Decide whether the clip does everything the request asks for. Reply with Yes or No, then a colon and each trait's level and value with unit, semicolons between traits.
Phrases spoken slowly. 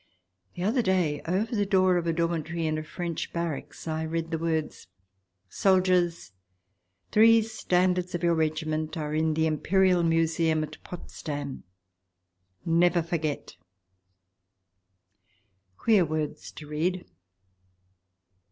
Yes: slow, 125 wpm